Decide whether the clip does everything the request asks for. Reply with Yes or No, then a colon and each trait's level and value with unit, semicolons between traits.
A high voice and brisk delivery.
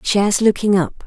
No: high, 200 Hz; average, 170 wpm